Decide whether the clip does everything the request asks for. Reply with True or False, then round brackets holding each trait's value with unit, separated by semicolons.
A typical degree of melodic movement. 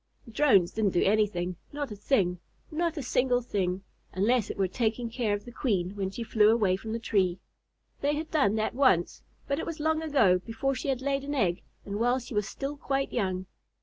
False (5.7 semitones)